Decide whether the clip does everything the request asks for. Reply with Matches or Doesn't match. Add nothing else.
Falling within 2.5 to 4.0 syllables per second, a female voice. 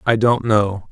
Doesn't match